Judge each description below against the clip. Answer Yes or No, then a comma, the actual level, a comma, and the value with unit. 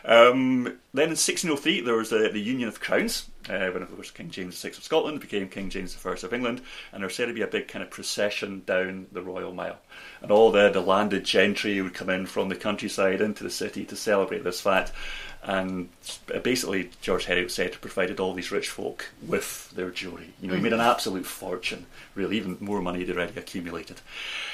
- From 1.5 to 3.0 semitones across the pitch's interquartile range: No, average, 3.7 semitones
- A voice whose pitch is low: Yes, very low, 95 Hz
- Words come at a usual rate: No, fast, 215 wpm